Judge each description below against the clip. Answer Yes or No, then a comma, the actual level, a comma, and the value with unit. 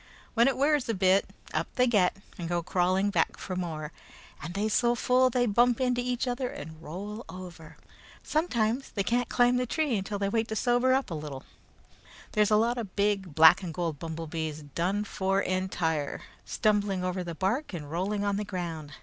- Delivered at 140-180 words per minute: No, average, 195 wpm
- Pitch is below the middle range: No, high, 200 Hz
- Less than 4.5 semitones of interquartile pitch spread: No, wide, 5.5 semitones